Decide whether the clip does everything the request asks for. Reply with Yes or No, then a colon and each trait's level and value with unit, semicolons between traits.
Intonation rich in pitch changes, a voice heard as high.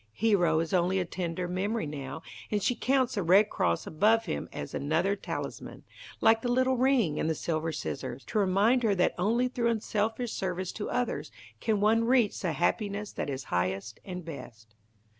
Yes: wide, 5.8 semitones; high, 195 Hz